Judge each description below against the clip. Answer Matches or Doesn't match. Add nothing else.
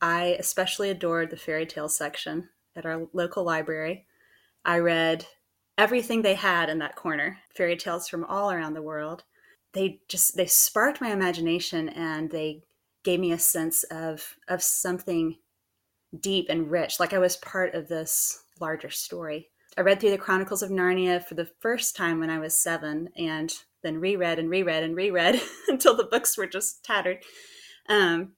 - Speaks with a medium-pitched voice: Matches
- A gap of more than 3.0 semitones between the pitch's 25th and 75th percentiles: Doesn't match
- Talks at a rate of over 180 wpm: Doesn't match